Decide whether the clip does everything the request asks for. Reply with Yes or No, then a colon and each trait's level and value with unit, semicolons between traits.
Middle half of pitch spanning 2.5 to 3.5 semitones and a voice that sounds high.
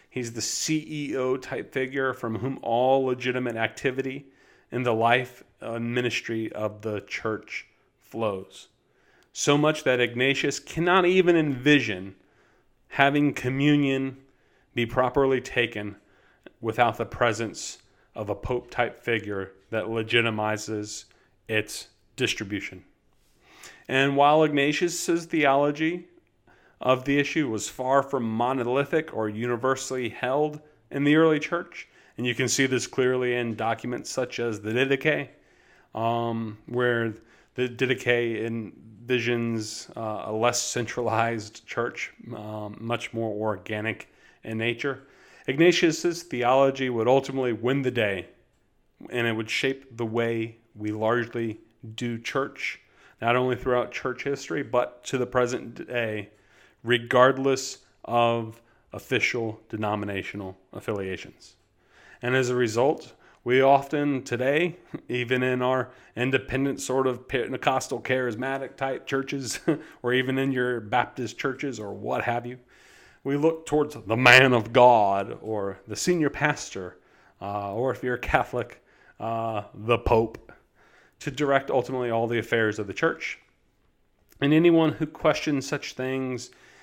No: average, 3.0 semitones; low, 125 Hz